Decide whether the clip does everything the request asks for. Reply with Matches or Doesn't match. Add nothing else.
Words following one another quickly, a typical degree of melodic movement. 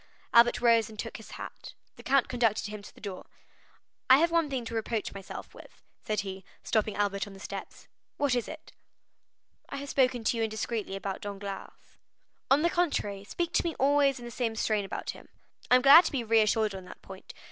Matches